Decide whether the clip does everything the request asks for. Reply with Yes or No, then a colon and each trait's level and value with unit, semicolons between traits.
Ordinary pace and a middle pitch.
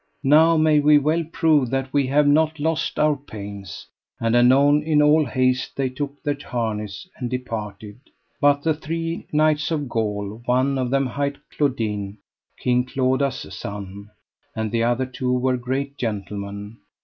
No: average, 155 wpm; low, 130 Hz